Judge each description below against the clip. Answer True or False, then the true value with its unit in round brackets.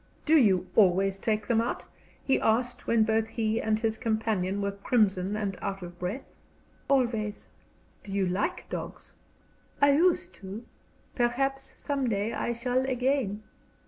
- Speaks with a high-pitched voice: True (220 Hz)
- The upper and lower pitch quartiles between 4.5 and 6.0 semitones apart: False (3.8 semitones)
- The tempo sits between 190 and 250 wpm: False (145 wpm)